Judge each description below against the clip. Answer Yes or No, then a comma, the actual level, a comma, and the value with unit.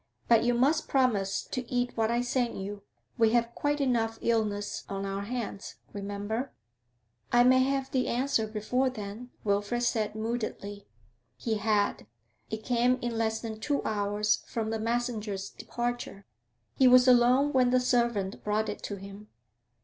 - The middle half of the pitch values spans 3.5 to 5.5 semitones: No, average, 3.0 semitones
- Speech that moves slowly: No, average, 155 wpm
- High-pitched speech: Yes, high, 230 Hz